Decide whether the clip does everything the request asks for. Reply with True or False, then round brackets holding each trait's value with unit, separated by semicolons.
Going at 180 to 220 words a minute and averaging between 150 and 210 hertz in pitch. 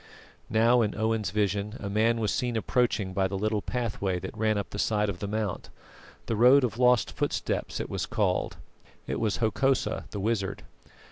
False (185 wpm; 110 Hz)